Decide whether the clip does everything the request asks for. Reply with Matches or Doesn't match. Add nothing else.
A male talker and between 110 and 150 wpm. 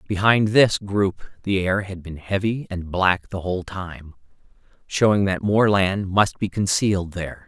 Doesn't match